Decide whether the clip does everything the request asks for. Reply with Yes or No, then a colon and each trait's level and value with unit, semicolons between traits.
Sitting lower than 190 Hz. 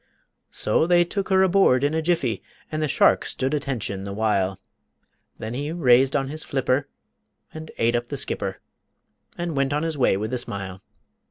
Yes: low, 135 Hz